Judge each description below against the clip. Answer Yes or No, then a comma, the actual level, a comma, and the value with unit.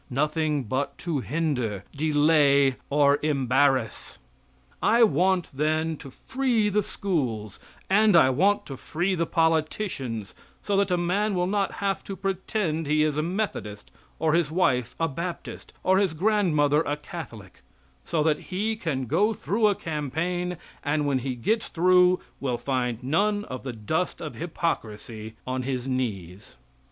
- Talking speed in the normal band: Yes, average, 150 wpm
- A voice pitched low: No, medium, 155 Hz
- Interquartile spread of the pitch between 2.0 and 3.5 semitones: No, wide, 5.6 semitones